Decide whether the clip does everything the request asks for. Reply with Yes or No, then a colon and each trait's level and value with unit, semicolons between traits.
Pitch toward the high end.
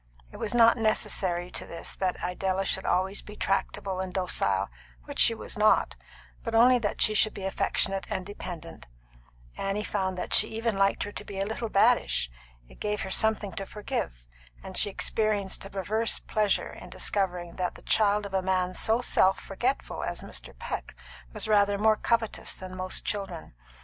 Yes: high, 195 Hz